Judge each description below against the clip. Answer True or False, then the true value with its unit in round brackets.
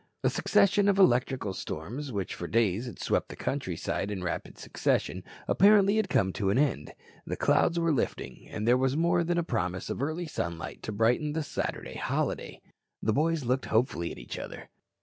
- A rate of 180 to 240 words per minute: True (190 wpm)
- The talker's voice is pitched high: False (130 Hz)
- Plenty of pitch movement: True (8.5 semitones)